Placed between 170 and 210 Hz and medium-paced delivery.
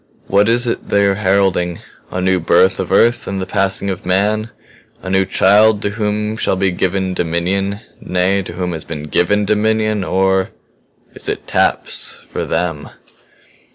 No: very low, 95 Hz; average, 165 wpm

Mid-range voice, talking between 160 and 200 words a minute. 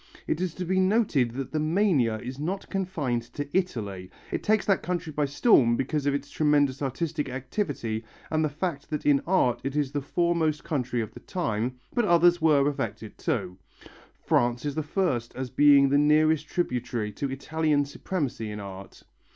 Yes: medium, 145 Hz; average, 180 wpm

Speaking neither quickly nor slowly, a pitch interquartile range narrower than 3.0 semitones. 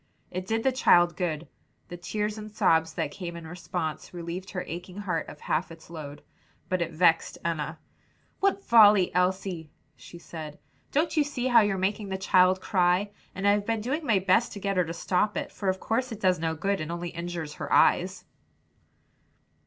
No: average, 190 wpm; average, 3.6 semitones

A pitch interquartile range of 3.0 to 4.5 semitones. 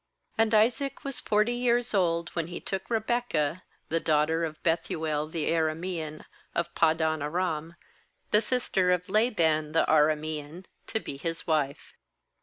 No: average, 5.2 semitones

